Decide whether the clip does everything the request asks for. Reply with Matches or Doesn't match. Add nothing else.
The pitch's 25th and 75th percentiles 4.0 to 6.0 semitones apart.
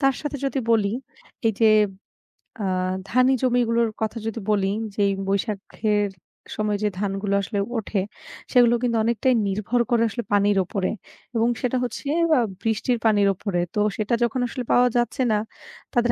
Doesn't match